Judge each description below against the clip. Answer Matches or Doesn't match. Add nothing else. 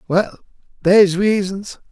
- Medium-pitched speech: Doesn't match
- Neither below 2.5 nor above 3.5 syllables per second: Matches